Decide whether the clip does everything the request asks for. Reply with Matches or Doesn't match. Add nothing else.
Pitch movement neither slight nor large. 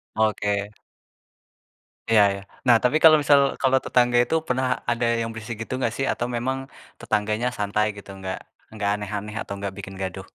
Matches